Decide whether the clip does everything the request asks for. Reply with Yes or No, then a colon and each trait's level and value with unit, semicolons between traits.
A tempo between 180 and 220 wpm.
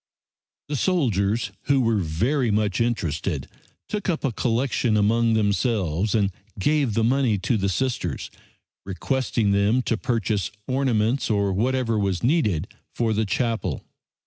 No: slow, 135 wpm